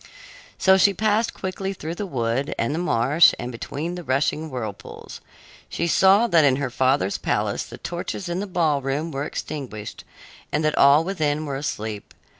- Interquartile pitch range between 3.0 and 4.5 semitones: No, average, 5.1 semitones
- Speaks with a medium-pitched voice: Yes, medium, 150 Hz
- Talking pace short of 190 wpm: Yes, average, 170 wpm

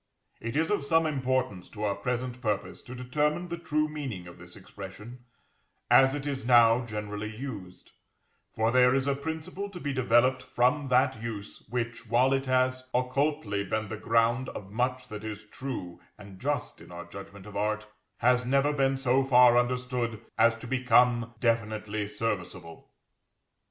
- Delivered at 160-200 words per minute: Yes, average, 165 wpm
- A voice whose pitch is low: Yes, low, 125 Hz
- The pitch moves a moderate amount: Yes, average, 3.6 semitones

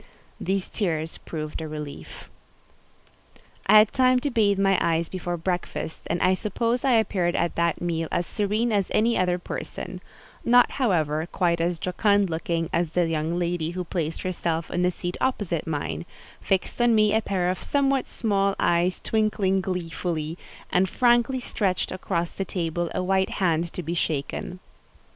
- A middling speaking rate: Yes, average, 165 wpm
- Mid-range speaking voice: Yes, medium, 180 Hz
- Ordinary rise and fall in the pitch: Yes, average, 3.5 semitones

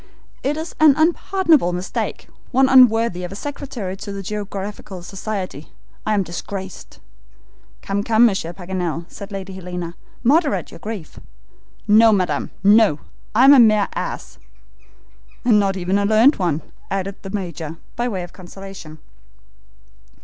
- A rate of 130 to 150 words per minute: Yes, average, 140 wpm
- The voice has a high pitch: Yes, high, 200 Hz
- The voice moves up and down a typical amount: Yes, average, 3.8 semitones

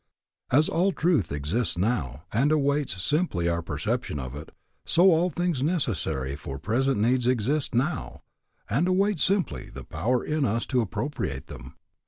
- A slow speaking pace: No, average, 155 wpm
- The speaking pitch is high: No, low, 125 Hz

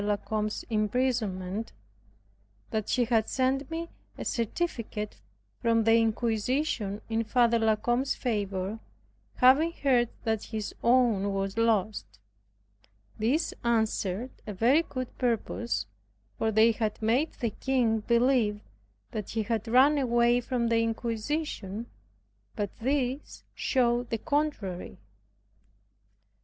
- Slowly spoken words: Yes, slow, 115 wpm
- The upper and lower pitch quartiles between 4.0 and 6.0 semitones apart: No, average, 3.0 semitones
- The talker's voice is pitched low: No, high, 230 Hz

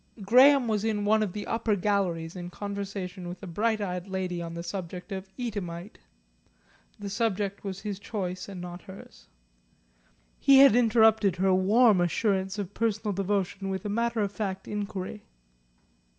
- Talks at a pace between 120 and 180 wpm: Yes, average, 160 wpm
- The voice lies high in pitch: Yes, high, 200 Hz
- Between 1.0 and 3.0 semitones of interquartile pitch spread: Yes, narrow, 2.6 semitones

